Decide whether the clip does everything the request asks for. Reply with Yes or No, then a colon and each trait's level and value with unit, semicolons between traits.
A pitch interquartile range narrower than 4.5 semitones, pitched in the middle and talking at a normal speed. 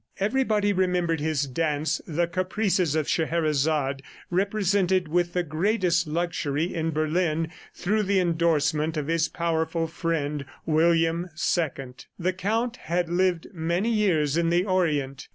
No: average, 2.8 semitones; medium, 170 Hz; slow, 130 wpm